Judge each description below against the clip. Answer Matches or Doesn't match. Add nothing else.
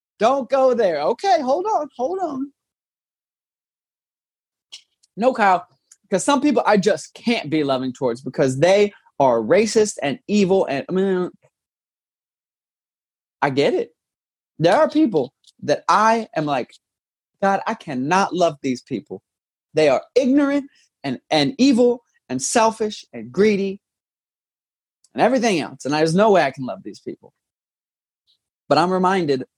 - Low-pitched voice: Doesn't match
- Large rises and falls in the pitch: Matches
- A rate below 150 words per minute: Matches